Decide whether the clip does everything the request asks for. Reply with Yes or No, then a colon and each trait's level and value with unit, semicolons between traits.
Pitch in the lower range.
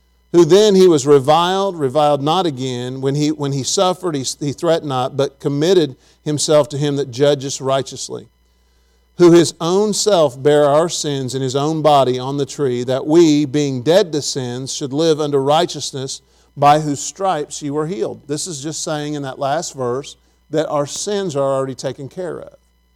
No: medium, 145 Hz